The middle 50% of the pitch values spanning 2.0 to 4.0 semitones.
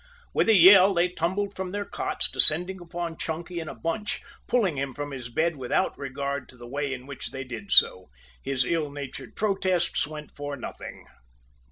No: average, 4.9 semitones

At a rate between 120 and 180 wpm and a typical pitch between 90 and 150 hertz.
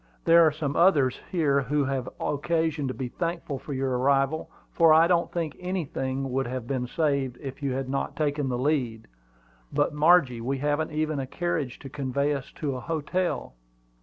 No: average, 190 wpm; medium, 140 Hz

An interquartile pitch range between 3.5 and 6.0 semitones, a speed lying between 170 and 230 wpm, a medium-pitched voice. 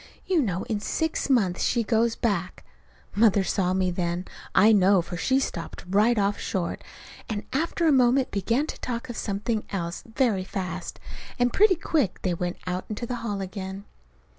No: average, 4.5 semitones; average, 180 wpm; high, 205 Hz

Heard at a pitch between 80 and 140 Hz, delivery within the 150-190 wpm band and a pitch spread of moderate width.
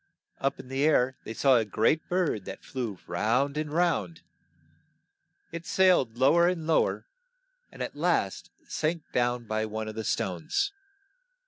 No: low, 135 Hz; average, 160 wpm; wide, 6.6 semitones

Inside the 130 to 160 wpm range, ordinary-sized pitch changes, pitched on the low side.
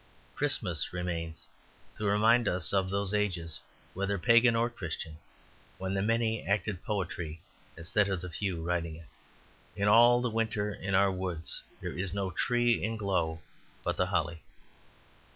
Yes: average, 150 wpm; average, 4.0 semitones; very low, 95 Hz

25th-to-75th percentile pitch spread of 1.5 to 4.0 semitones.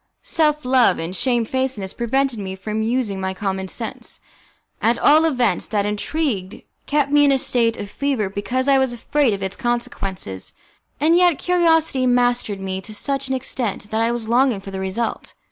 No: average, 5.2 semitones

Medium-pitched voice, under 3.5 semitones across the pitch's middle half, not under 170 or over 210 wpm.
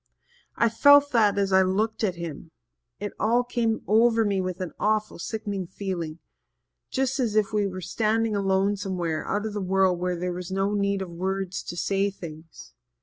No: high, 195 Hz; average, 2.8 semitones; average, 185 wpm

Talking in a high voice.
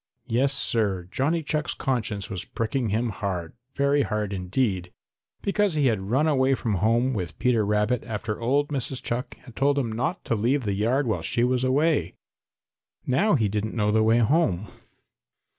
No: low, 120 Hz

